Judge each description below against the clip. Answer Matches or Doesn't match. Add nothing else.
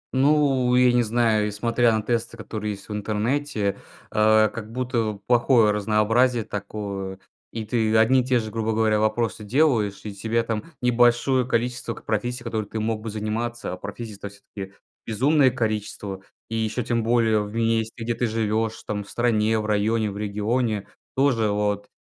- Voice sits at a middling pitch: Doesn't match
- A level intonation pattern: Matches